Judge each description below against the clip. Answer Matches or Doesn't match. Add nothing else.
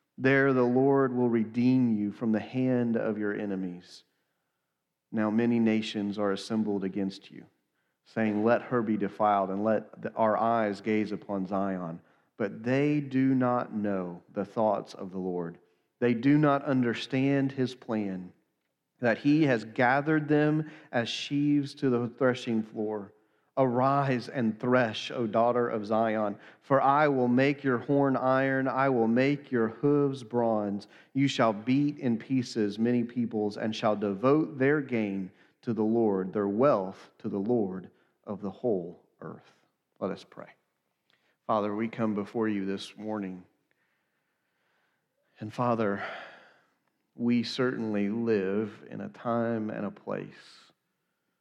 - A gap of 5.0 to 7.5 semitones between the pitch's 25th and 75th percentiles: Doesn't match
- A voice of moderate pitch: Doesn't match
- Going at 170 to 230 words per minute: Doesn't match